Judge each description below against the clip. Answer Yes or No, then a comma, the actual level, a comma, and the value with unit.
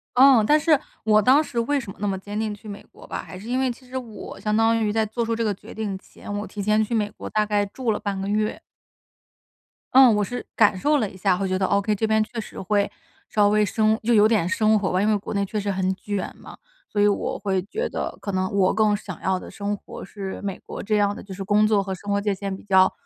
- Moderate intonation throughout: No, narrow, 1.8 semitones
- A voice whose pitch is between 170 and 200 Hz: No, high, 210 Hz